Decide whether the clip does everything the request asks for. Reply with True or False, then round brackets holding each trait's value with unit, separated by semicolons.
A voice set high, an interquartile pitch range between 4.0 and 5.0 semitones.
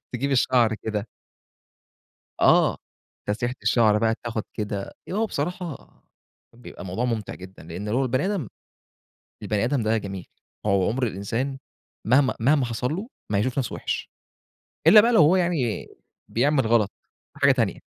False (120 Hz; 4.7 semitones)